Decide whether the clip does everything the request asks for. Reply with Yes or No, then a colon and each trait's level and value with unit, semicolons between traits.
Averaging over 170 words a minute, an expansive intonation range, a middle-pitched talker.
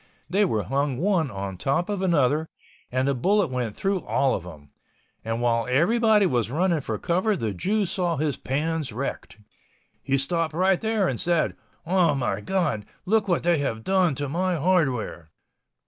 Yes: average, 180 wpm; wide, 6.7 semitones; medium, 155 Hz